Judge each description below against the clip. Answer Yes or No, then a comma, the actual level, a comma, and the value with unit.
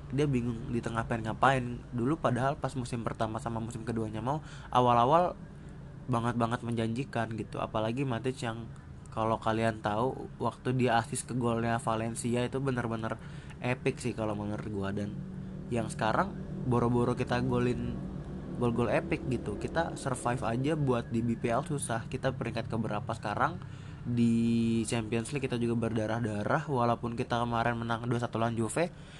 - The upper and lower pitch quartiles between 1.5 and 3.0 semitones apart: Yes, narrow, 2.6 semitones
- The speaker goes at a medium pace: No, fast, 150 wpm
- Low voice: Yes, low, 120 Hz